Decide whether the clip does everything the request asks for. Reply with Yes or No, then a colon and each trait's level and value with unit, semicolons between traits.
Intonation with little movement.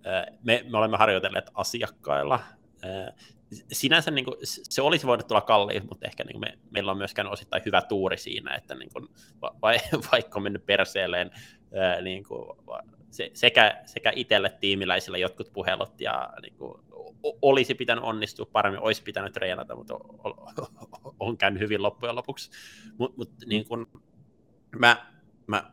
No: average, 3.0 semitones